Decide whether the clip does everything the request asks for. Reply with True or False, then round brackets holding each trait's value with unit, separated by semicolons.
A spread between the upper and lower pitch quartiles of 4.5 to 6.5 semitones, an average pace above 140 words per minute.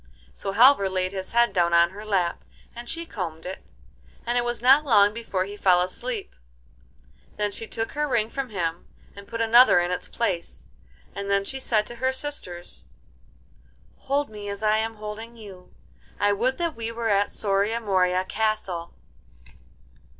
False (3.9 semitones; 170 wpm)